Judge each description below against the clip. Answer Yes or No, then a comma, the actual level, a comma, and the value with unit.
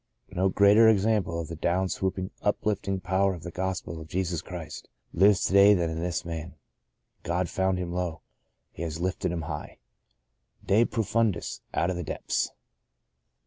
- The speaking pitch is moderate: No, very low, 90 Hz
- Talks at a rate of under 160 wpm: No, average, 165 wpm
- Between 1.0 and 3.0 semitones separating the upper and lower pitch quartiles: Yes, narrow, 2.5 semitones